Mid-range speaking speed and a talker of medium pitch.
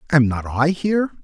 Yes: average, 195 wpm; medium, 150 Hz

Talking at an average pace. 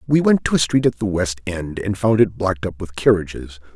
No: fast, 255 wpm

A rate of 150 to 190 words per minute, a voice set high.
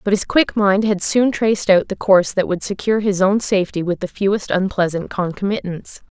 No: fast, 205 wpm; high, 195 Hz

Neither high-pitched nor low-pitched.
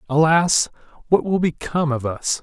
Yes: medium, 155 Hz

